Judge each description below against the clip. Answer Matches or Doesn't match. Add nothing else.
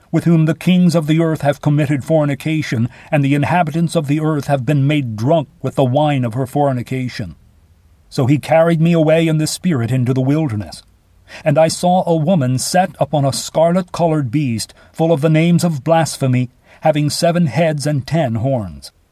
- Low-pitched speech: Doesn't match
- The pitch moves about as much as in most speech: Matches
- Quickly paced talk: Doesn't match